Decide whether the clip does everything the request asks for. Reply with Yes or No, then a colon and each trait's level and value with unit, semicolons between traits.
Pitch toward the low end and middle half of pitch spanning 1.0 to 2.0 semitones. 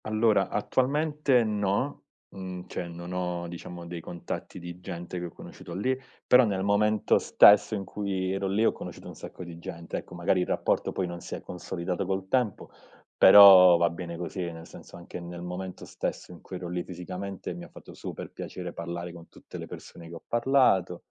No: very low, 90 Hz; average, 2.7 semitones